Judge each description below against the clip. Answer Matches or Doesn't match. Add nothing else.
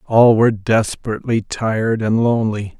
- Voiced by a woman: Doesn't match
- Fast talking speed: Doesn't match